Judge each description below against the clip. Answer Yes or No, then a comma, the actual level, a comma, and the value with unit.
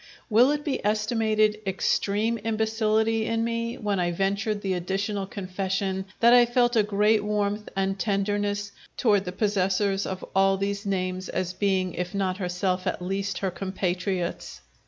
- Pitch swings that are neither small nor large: No, narrow, 2.1 semitones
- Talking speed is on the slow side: No, average, 155 wpm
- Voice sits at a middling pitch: No, high, 200 Hz